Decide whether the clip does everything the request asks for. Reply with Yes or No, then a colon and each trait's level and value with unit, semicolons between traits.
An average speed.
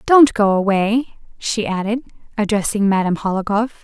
No: slow, 125 wpm